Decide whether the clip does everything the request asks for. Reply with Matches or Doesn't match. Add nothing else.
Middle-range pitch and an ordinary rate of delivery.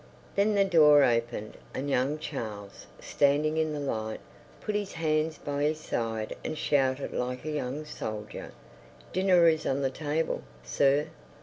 Matches